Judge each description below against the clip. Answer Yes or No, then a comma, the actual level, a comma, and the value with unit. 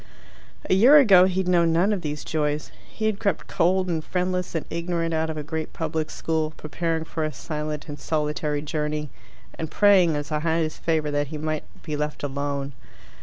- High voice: No, medium, 160 Hz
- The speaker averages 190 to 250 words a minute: Yes, average, 195 wpm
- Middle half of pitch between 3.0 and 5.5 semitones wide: No, narrow, 2.6 semitones